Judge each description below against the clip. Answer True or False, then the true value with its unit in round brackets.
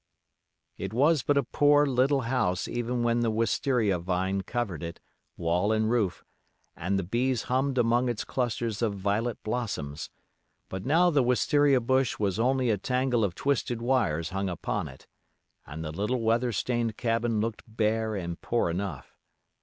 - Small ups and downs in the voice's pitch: False (4.4 semitones)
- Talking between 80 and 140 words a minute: False (160 wpm)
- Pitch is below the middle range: True (115 Hz)